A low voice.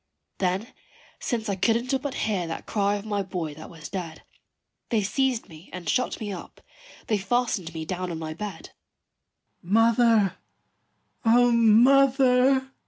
No: high, 210 Hz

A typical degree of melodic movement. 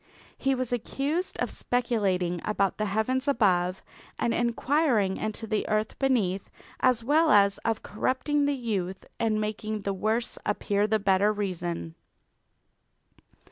Yes: average, 3.9 semitones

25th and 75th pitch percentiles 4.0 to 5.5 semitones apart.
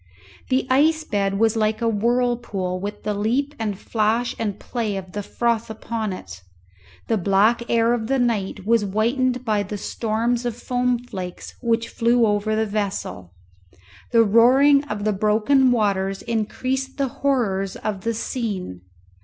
No: average, 3.0 semitones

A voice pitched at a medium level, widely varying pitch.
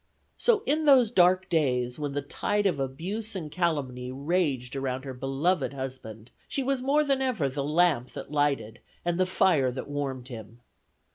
Yes: medium, 145 Hz; wide, 6.1 semitones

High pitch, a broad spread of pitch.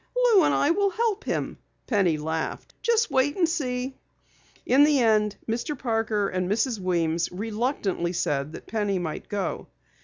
Yes: high, 225 Hz; wide, 7.8 semitones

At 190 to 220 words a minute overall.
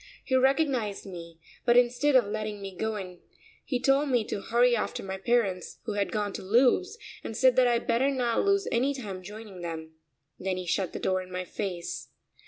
Yes: average, 200 wpm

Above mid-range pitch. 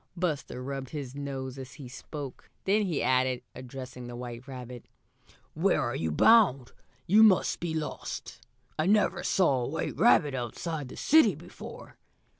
No: medium, 140 Hz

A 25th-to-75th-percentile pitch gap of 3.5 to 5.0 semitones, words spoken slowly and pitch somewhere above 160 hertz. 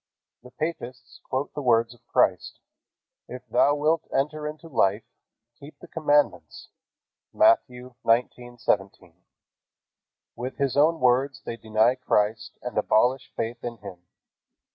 No: average, 4.0 semitones; slow, 120 wpm; low, 125 Hz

